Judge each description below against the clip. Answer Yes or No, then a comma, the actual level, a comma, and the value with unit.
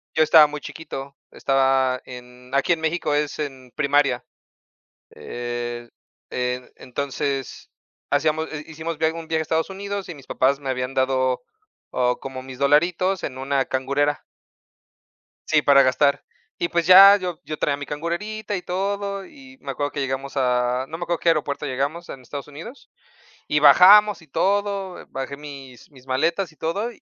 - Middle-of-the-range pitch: Yes, medium, 145 Hz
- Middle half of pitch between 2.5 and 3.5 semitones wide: No, average, 4.4 semitones